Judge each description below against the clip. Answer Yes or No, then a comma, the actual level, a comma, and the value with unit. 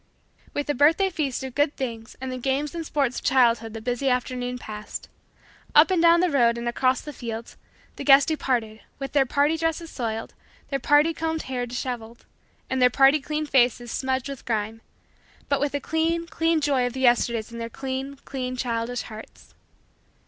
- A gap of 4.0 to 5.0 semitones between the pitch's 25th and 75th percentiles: No, average, 3.4 semitones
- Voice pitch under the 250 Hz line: No, very high, 260 Hz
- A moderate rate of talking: Yes, average, 185 wpm